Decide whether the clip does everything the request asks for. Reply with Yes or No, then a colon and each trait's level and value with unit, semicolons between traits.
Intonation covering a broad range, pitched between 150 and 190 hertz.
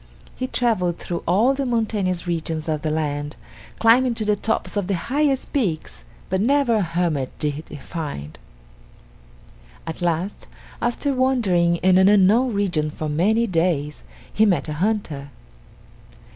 Yes: wide, 6.1 semitones; medium, 185 Hz